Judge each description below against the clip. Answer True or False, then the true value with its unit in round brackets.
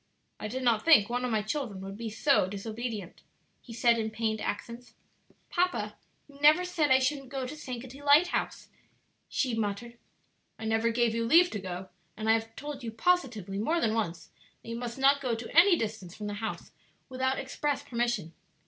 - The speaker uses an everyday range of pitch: True (3.9 semitones)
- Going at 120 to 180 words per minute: False (190 wpm)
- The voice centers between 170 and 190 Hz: False (235 Hz)